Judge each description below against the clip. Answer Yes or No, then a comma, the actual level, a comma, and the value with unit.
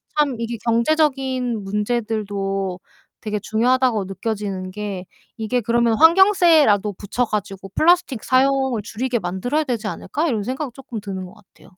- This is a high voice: Yes, high, 230 Hz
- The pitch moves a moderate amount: Yes, average, 4.3 semitones